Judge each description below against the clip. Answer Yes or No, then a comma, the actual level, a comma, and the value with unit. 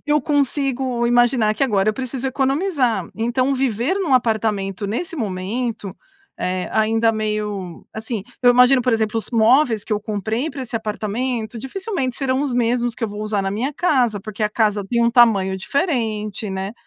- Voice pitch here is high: Yes, high, 230 Hz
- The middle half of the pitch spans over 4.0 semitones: No, average, 3.6 semitones